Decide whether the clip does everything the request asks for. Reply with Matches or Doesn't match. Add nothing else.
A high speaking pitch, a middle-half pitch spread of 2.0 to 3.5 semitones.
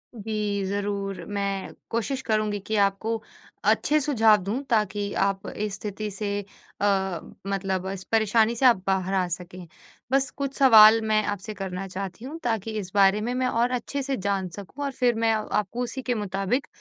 Matches